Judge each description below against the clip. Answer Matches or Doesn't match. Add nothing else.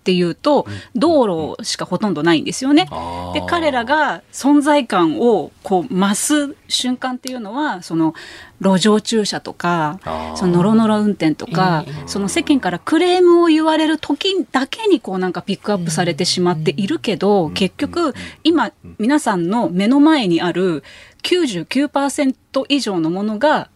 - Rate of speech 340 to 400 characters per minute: Doesn't match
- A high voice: Matches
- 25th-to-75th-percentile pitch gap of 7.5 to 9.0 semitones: Matches